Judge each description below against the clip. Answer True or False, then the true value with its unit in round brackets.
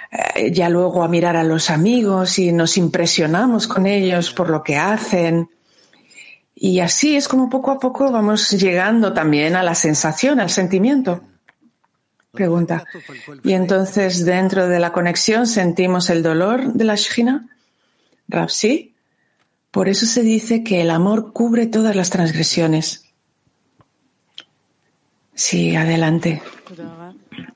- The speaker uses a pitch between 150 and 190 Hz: True (185 Hz)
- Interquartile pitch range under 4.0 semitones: False (4.5 semitones)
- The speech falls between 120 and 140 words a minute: True (130 wpm)